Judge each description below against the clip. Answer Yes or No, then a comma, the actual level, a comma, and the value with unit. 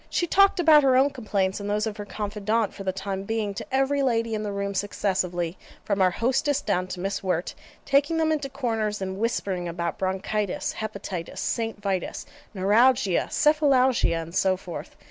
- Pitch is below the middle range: No, high, 210 Hz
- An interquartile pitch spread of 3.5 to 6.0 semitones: Yes, average, 5.2 semitones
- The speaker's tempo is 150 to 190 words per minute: Yes, average, 180 wpm